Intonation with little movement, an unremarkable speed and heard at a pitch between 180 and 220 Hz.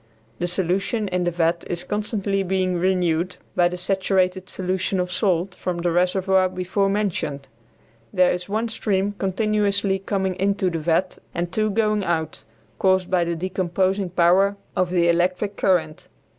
Yes: narrow, 1.9 semitones; average, 155 wpm; medium, 185 Hz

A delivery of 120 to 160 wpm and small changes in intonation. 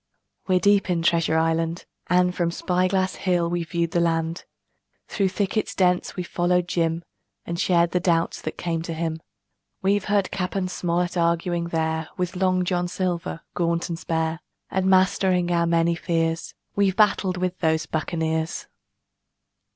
Yes: average, 155 wpm; narrow, 1.7 semitones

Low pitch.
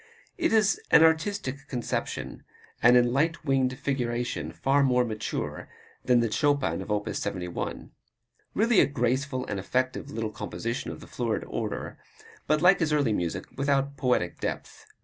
Yes: low, 130 Hz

